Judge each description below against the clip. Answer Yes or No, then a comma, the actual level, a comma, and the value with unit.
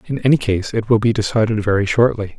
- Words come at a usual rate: No, fast, 225 wpm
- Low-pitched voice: Yes, low, 110 Hz